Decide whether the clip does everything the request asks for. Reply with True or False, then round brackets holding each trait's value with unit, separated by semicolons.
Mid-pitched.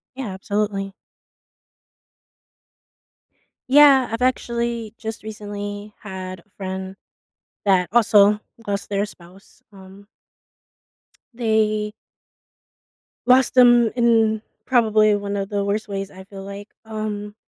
False (210 Hz)